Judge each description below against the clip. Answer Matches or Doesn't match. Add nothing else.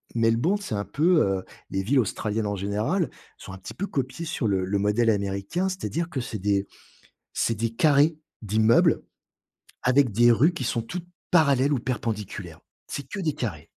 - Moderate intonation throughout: Doesn't match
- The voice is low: Matches